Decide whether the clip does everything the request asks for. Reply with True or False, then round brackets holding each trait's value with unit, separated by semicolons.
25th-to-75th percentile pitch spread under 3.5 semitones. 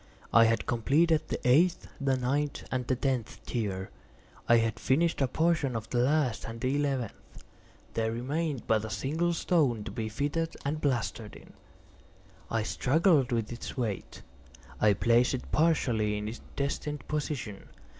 False (4.5 semitones)